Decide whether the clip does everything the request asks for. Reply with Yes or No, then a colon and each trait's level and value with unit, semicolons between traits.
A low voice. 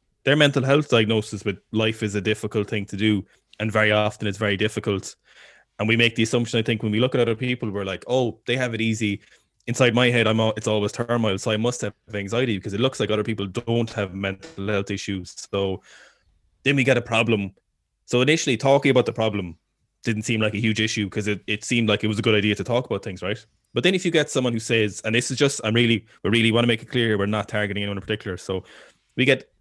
Yes: low, 110 Hz